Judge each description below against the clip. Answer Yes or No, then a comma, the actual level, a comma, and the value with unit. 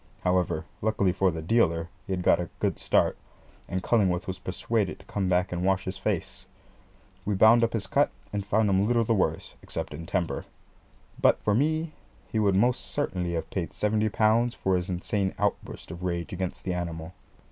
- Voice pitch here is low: Yes, very low, 95 Hz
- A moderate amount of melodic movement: Yes, average, 3.4 semitones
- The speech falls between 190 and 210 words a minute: Yes, average, 195 wpm